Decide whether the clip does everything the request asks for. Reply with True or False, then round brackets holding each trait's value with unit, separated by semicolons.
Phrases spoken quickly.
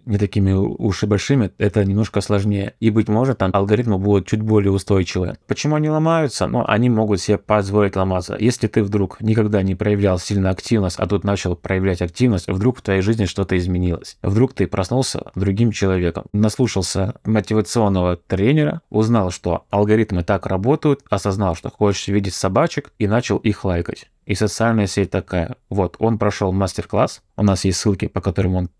True (175 wpm)